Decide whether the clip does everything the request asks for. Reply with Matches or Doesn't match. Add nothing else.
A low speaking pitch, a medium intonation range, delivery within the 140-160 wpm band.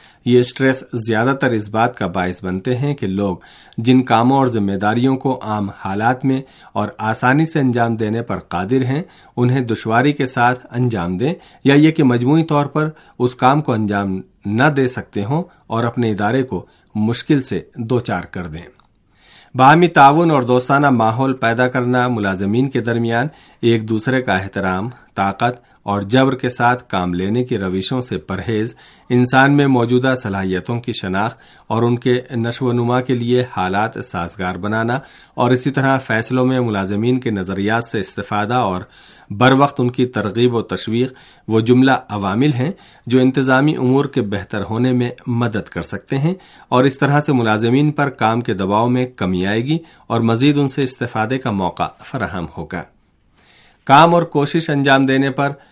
Doesn't match